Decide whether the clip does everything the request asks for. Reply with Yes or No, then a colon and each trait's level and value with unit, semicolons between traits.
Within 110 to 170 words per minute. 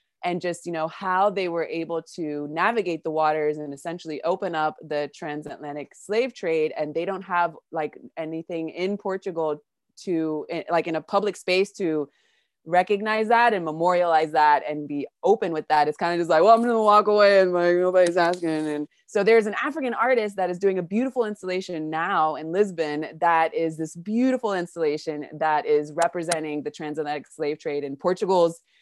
No: average, 185 wpm